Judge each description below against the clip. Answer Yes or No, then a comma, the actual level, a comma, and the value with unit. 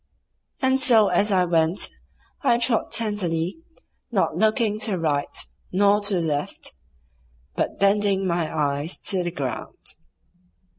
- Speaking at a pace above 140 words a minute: No, slow, 135 wpm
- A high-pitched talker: Yes, high, 195 Hz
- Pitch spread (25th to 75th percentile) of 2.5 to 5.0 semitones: Yes, average, 4.4 semitones